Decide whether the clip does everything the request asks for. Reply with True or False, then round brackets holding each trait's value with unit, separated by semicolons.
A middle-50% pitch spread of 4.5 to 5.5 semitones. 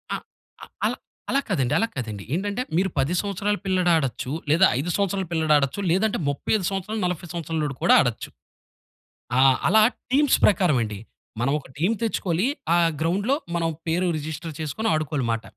True (5.2 semitones)